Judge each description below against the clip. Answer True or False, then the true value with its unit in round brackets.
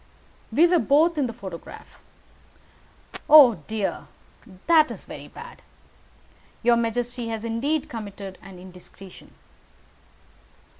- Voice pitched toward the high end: True (235 Hz)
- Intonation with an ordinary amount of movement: False (6.9 semitones)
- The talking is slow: True (105 wpm)